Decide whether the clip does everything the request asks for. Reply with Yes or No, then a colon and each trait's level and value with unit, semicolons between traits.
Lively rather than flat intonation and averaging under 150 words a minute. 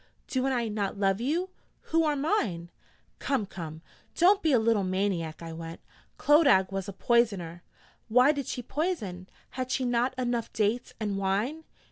No: wide, 5.9 semitones; average, 160 wpm